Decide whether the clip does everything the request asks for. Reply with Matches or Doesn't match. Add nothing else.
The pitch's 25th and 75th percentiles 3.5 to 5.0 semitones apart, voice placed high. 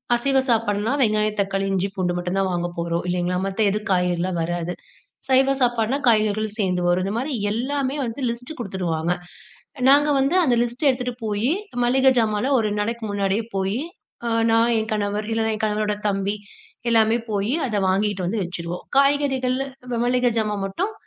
Matches